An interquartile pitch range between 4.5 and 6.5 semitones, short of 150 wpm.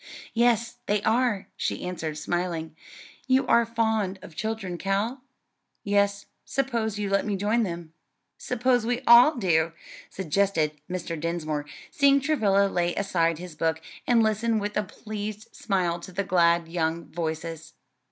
Yes: average, 4.8 semitones; average, 140 wpm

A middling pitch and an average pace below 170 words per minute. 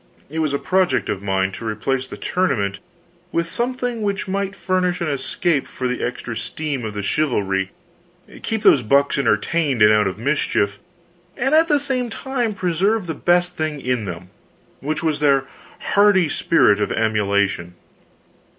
Yes: medium, 145 Hz; average, 160 wpm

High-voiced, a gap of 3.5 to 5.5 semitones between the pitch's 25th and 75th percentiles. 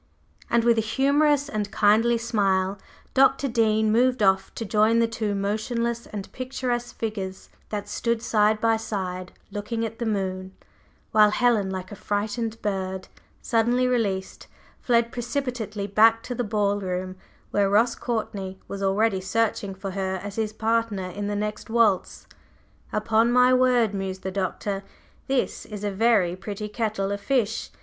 No: high, 215 Hz; average, 2.9 semitones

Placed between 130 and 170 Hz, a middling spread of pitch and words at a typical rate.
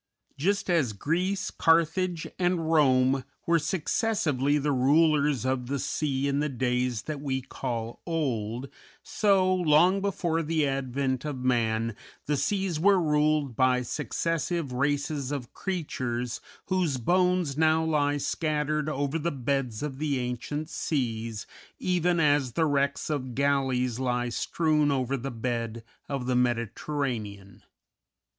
No: medium, 140 Hz; average, 4.2 semitones; slow, 130 wpm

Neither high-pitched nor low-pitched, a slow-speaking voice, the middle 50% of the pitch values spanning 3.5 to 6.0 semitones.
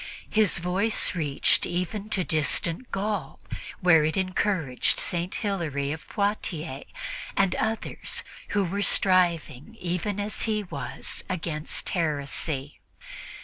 Yes: medium, 180 Hz; slow, 110 wpm; average, 4.5 semitones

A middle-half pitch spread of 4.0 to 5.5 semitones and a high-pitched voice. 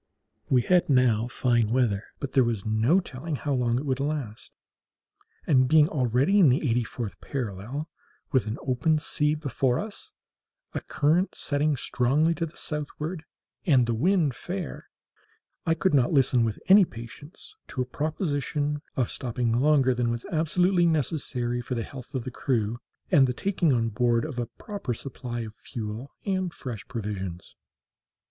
No: average, 4.5 semitones; low, 130 Hz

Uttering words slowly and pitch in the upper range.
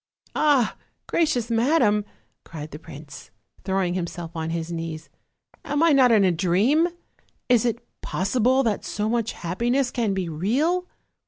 No: average, 150 wpm; high, 210 Hz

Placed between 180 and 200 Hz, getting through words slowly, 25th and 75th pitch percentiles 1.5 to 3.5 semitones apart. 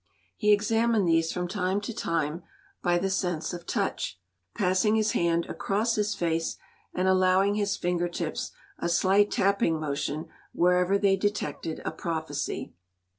No: medium, 185 Hz; average, 145 wpm; average, 3.2 semitones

